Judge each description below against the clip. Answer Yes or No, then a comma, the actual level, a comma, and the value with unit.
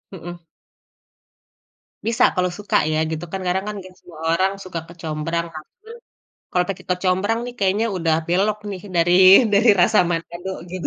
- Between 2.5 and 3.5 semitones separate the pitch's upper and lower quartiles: Yes, average, 2.8 semitones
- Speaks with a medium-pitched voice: Yes, medium, 180 Hz